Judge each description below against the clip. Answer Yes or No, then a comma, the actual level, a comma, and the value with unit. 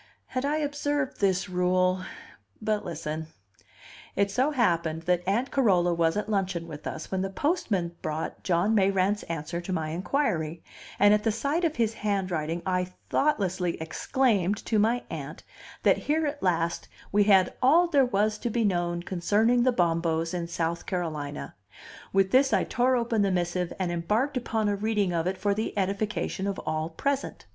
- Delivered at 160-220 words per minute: Yes, average, 170 wpm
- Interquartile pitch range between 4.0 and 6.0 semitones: Yes, average, 4.8 semitones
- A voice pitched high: Yes, high, 195 Hz